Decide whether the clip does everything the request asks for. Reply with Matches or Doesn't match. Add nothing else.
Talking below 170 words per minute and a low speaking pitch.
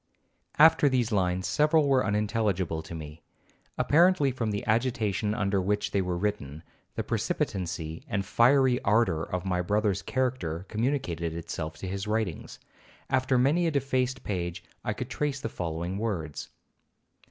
Matches